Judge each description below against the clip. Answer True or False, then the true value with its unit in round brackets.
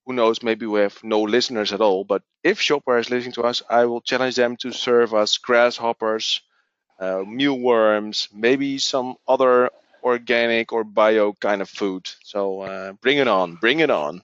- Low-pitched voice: True (115 Hz)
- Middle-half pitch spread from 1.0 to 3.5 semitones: True (2.8 semitones)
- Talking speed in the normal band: True (180 wpm)